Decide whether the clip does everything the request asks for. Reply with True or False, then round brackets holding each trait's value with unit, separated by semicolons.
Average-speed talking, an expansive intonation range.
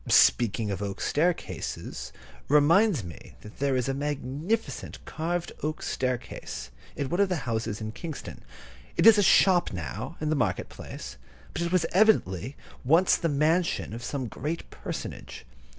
True (155 wpm; 6.9 semitones)